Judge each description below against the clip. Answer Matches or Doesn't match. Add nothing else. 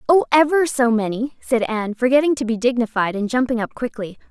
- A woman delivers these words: Matches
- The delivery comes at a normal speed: Matches